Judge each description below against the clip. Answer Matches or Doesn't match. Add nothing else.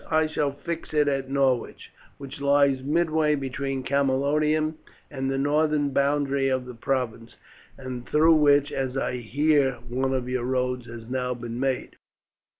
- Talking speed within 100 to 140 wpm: Doesn't match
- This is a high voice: Doesn't match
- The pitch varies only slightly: Matches